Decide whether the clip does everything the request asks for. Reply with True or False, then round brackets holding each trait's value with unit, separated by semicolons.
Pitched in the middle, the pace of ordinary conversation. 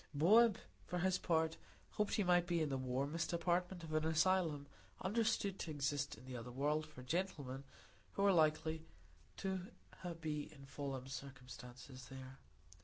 True (155 Hz; 155 wpm)